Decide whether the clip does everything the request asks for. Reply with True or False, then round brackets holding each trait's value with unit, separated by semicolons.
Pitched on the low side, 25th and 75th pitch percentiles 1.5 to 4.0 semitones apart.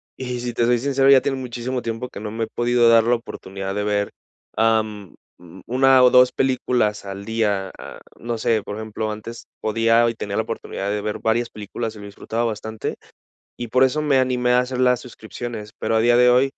True (115 Hz; 2.5 semitones)